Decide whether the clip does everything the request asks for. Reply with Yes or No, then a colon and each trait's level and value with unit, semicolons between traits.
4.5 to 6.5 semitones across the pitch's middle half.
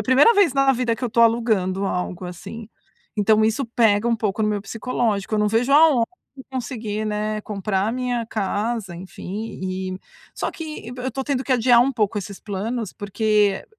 No: average, 3.2 semitones